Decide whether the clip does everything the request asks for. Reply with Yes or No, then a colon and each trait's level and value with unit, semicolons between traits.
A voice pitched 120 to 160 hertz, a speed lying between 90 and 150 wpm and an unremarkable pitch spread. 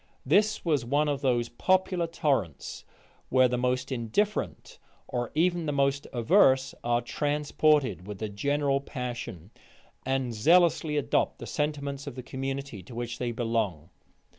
Yes: low, 135 Hz; average, 140 wpm; average, 3.8 semitones